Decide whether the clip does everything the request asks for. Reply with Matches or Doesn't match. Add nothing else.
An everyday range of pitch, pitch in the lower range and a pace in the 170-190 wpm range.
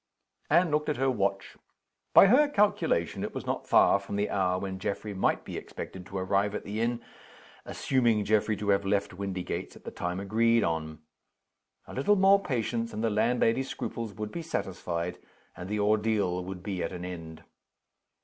Matches